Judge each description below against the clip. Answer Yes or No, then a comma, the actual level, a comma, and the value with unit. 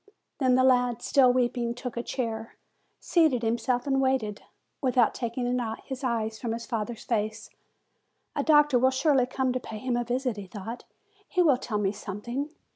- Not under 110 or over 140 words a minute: No, average, 175 wpm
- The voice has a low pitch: No, high, 245 Hz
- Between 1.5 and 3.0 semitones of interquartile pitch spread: Yes, narrow, 2.4 semitones